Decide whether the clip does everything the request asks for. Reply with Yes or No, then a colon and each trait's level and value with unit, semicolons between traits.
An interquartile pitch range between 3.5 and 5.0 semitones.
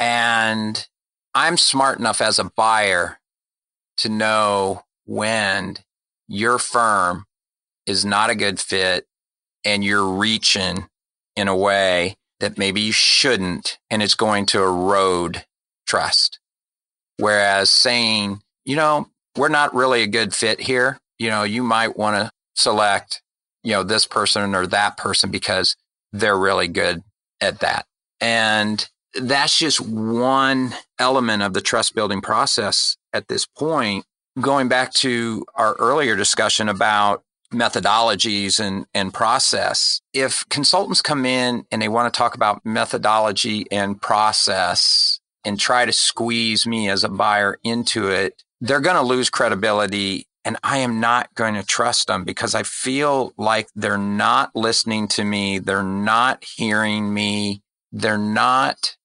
No: average, 2.8 semitones